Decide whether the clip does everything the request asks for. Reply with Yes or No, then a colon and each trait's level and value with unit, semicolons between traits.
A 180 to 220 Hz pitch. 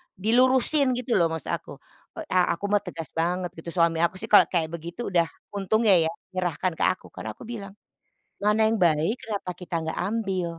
Yes: medium, 185 Hz